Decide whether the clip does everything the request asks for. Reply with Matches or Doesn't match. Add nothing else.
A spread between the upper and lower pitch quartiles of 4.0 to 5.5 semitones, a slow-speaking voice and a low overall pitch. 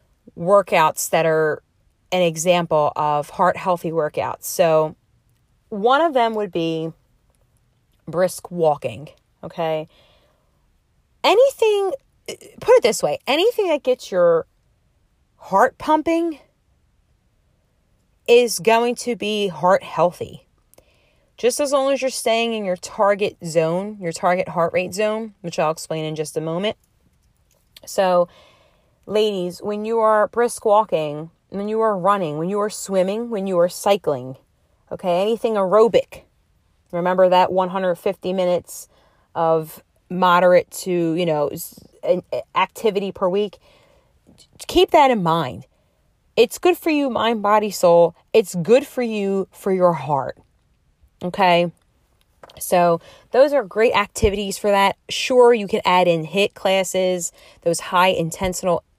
Doesn't match